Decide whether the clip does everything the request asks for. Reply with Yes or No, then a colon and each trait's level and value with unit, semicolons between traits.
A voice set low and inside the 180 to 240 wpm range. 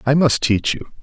Yes: low, 130 Hz; fast, 235 wpm